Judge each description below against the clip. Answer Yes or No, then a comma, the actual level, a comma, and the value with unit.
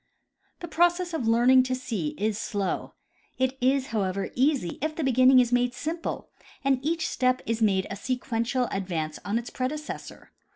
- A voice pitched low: No, very high, 255 Hz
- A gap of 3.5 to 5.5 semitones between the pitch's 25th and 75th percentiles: Yes, average, 3.9 semitones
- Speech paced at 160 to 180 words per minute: Yes, average, 165 wpm